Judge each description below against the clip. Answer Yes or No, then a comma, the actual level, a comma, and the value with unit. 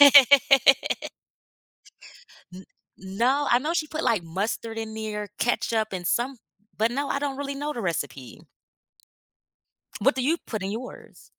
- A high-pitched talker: Yes, high, 240 Hz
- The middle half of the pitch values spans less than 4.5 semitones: No, average, 4.8 semitones